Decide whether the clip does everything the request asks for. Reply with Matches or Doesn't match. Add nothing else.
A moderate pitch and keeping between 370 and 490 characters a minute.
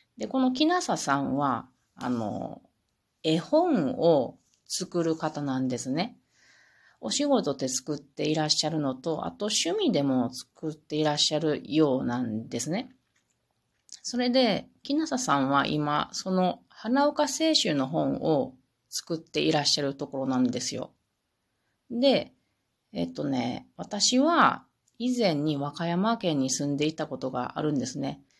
Doesn't match